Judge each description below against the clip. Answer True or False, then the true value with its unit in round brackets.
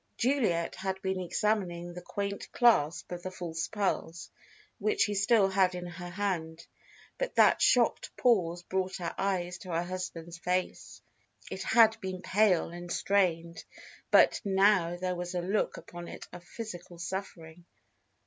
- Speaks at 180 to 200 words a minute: False (150 wpm)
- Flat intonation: True (2.3 semitones)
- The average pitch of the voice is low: False (180 Hz)